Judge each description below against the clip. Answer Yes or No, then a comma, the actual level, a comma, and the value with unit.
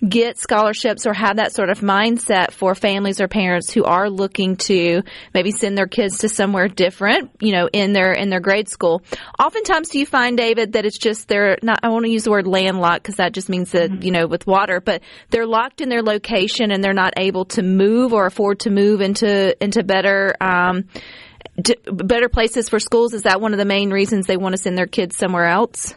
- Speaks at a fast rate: Yes, fast, 220 wpm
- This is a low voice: No, high, 200 Hz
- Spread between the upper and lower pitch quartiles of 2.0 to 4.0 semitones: Yes, average, 3.0 semitones